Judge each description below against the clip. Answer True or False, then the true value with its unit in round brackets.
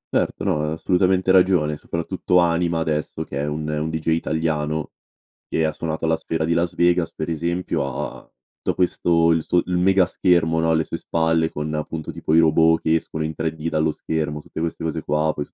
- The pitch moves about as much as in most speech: False (1.4 semitones)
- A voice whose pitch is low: True (80 Hz)